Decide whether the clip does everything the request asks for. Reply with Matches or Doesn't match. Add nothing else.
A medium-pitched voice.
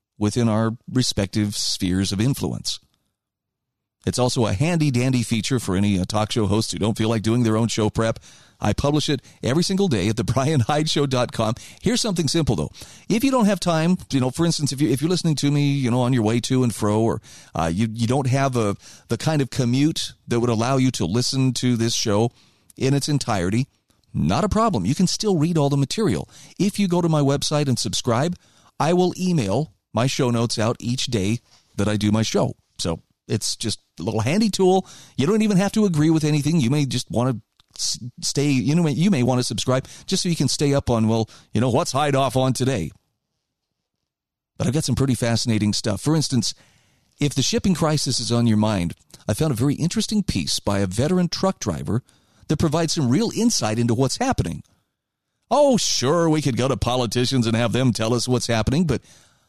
Doesn't match